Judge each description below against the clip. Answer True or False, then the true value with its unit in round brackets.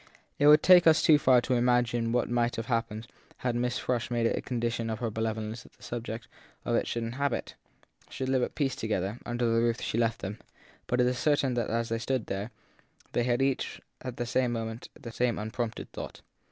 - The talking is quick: True (220 wpm)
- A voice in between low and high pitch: False (120 Hz)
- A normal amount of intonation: False (1.6 semitones)